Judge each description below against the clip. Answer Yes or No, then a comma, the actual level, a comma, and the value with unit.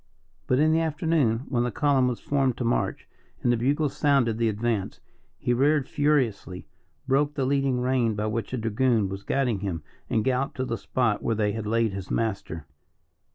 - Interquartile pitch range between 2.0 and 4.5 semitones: Yes, average, 3.9 semitones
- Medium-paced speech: Yes, average, 190 wpm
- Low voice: Yes, low, 120 Hz